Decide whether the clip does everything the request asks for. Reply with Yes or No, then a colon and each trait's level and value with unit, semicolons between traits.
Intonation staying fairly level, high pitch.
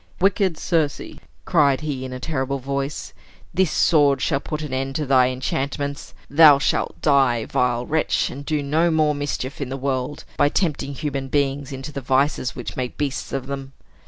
No: narrow, 2.1 semitones; medium, 140 Hz